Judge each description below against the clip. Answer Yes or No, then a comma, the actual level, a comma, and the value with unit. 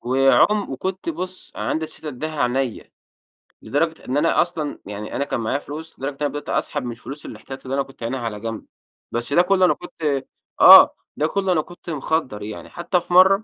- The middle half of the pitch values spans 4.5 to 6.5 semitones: Yes, average, 4.9 semitones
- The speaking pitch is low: No, medium, 145 Hz